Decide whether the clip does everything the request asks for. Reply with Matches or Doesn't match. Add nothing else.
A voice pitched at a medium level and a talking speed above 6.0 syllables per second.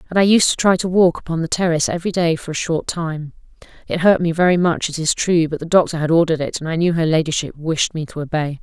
Matches